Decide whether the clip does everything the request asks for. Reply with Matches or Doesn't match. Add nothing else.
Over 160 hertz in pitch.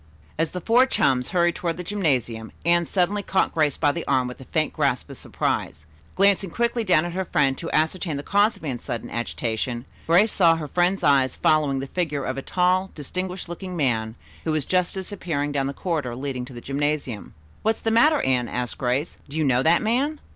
Doesn't match